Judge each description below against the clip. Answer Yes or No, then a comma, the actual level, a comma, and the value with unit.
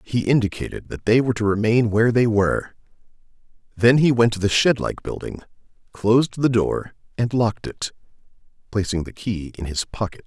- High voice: No, low, 110 Hz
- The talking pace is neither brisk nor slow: Yes, average, 175 wpm